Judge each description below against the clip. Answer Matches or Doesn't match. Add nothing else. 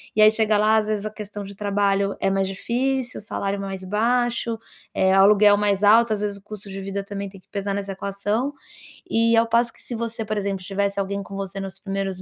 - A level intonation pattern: Matches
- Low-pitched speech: Doesn't match